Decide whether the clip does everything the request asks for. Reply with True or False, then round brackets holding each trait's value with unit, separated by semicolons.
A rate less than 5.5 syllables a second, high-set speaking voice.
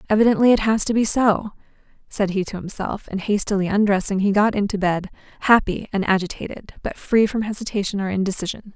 False (5.9 syllables/s; 205 Hz)